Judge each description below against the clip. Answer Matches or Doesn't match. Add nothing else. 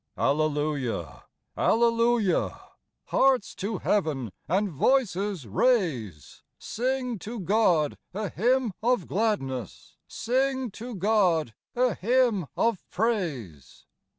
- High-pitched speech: Matches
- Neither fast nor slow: Doesn't match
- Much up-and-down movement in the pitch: Matches